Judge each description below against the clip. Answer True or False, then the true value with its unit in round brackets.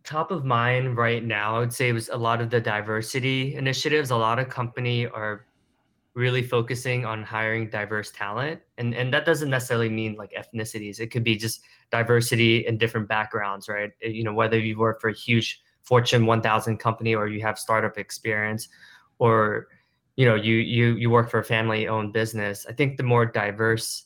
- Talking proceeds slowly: False (195 wpm)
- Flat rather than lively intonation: True (1.7 semitones)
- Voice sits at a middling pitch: False (115 Hz)